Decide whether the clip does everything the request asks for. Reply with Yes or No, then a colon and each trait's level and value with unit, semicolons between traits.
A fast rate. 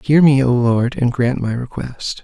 Yes: fast, 215 wpm